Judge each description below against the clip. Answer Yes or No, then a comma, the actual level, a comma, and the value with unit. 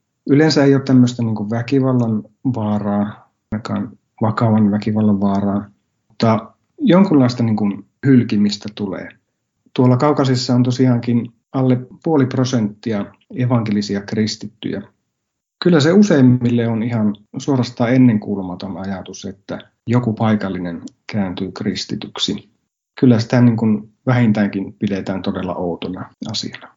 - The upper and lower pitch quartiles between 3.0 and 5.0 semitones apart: Yes, average, 3.6 semitones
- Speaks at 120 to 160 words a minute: No, average, 105 wpm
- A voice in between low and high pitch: No, low, 110 Hz